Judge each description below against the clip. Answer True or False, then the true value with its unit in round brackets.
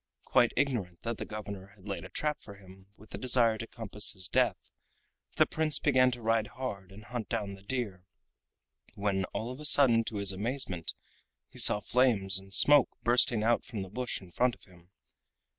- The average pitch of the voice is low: True (110 Hz)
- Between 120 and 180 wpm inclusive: False (195 wpm)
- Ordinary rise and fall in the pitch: True (4.2 semitones)